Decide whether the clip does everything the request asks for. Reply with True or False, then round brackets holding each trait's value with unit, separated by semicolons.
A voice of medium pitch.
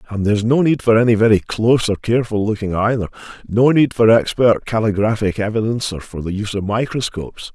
False (110 Hz)